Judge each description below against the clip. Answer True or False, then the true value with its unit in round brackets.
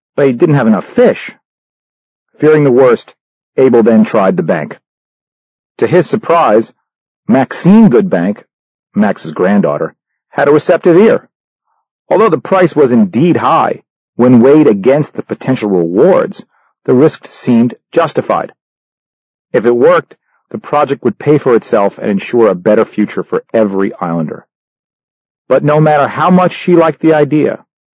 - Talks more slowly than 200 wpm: True (140 wpm)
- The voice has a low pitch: False (145 Hz)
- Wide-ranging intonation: True (6.1 semitones)